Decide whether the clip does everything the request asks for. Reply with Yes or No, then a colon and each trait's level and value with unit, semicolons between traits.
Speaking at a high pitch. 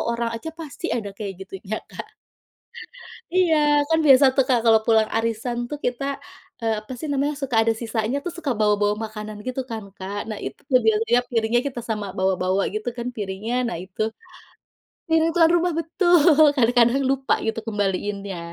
Yes: high, 230 Hz